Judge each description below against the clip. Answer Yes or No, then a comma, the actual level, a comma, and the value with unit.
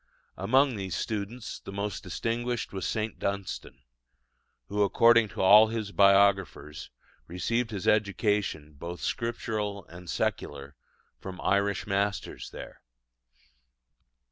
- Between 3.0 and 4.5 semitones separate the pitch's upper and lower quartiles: No, narrow, 2.6 semitones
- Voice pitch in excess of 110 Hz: No, low, 100 Hz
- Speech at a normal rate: No, slow, 110 wpm